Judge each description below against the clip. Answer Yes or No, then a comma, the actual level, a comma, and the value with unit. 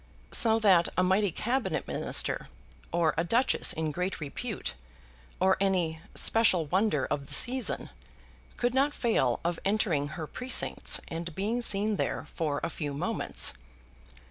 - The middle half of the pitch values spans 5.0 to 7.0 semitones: Yes, wide, 5.6 semitones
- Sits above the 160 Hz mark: Yes, medium, 185 Hz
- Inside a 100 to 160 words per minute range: Yes, average, 145 wpm